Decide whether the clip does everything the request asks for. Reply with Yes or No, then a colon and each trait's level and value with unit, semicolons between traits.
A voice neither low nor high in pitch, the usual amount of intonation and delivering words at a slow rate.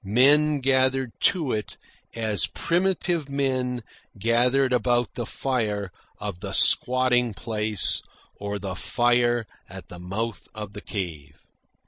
No: low, 120 Hz; average, 4.2 semitones; slow, 120 wpm